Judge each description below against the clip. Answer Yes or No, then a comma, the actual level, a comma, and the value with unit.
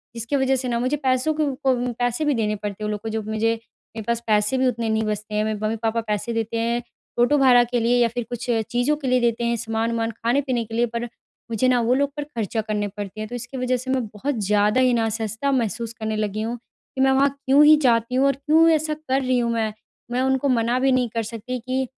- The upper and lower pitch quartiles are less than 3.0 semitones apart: Yes, narrow, 2.6 semitones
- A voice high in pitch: Yes, high, 235 Hz